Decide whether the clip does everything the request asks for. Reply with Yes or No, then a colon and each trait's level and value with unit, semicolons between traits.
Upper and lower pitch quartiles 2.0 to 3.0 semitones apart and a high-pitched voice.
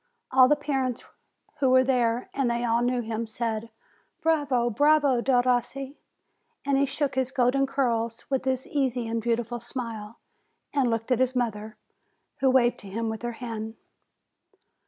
Yes: narrow, 2.5 semitones; high, 245 Hz